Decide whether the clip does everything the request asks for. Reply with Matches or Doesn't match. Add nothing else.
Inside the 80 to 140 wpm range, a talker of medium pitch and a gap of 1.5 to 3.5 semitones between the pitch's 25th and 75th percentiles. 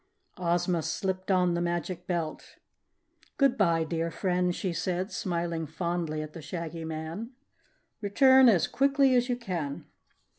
Matches